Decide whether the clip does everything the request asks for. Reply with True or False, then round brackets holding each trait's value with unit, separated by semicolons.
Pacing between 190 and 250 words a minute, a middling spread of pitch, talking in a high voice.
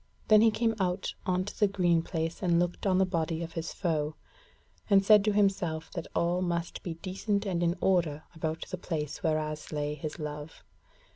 False (195 wpm; 3.2 semitones; 175 Hz)